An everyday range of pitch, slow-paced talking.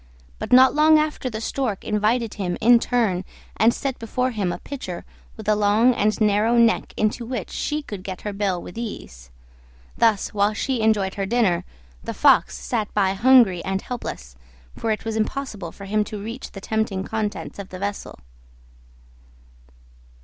No: average, 3.2 semitones; average, 170 wpm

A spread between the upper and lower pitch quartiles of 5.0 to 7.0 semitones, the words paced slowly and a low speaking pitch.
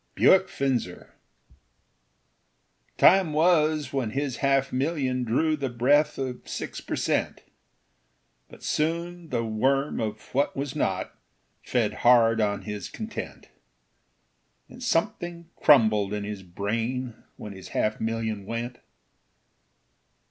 Yes: wide, 5.5 semitones; slow, 115 wpm; low, 130 Hz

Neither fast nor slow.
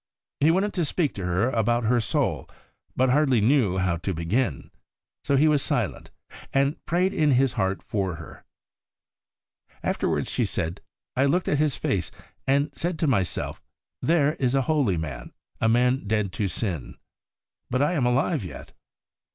Yes: average, 165 wpm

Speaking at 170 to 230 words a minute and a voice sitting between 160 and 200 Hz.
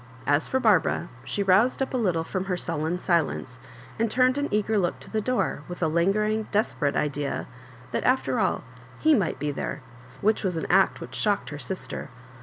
Yes: fast, 205 wpm; high, 190 Hz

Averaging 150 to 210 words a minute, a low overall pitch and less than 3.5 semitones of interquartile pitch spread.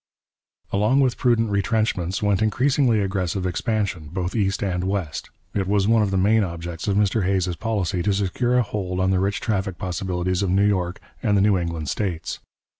Yes: average, 190 wpm; low, 100 Hz; narrow, 2.6 semitones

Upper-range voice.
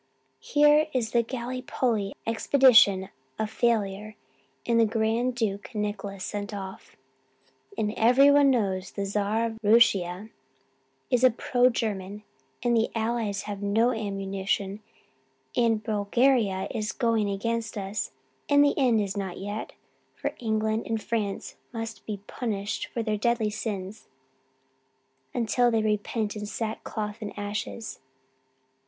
Yes: high, 220 Hz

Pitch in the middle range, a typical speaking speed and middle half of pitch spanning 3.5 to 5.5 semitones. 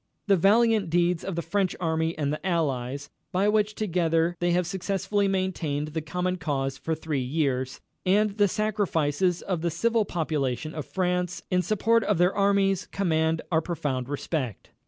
Yes: medium, 175 Hz; average, 165 wpm; average, 4.0 semitones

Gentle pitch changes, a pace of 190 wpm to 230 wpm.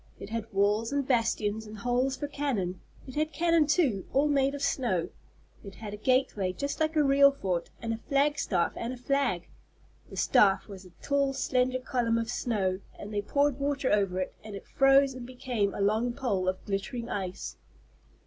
No: average, 5.3 semitones; average, 195 wpm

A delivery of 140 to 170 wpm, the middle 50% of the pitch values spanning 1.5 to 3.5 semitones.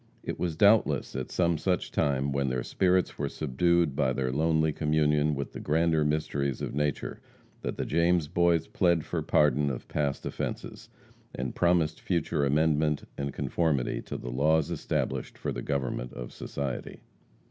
Yes: average, 160 wpm; average, 3.0 semitones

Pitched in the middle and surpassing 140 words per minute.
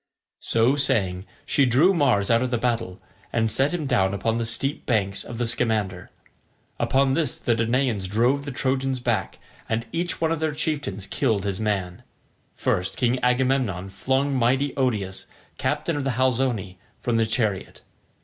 No: low, 120 Hz; average, 165 wpm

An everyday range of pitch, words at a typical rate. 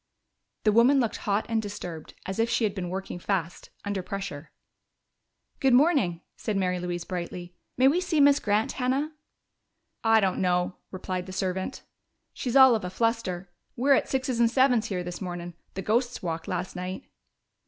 Yes: average, 5.0 semitones; average, 175 wpm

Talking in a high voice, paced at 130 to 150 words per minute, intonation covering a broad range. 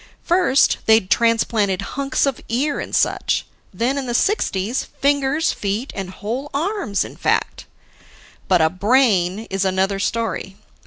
Yes: high, 230 Hz; average, 140 wpm; wide, 5.9 semitones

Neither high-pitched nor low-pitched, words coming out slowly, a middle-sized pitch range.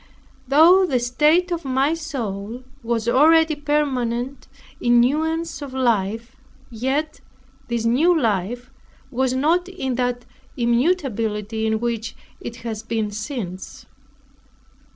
No: very high, 250 Hz; slow, 110 wpm; average, 4.6 semitones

